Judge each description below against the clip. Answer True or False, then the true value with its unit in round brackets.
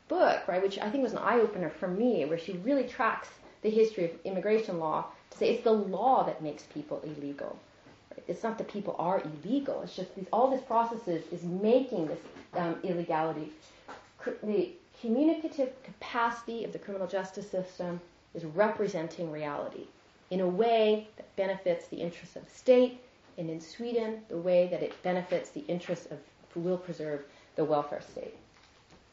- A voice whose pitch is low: False (190 Hz)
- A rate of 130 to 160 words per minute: False (180 wpm)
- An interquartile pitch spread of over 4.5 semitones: True (5.2 semitones)